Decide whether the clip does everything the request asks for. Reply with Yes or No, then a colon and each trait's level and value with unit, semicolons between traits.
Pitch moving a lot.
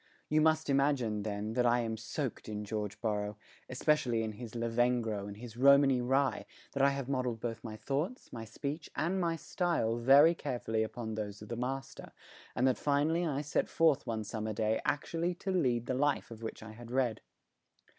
No: average, 4.2 semitones